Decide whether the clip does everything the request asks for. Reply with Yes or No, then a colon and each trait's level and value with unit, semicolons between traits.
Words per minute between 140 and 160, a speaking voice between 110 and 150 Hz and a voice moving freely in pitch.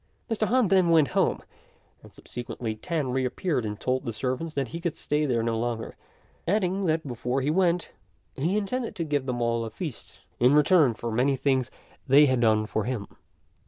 No: average, 190 wpm; low, 135 Hz; wide, 5.8 semitones